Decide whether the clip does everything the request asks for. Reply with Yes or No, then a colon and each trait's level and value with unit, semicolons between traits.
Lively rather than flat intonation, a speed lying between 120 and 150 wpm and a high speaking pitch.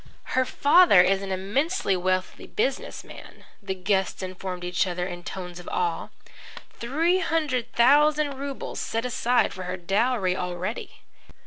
Yes: wide, 6.3 semitones; average, 140 wpm; high, 195 Hz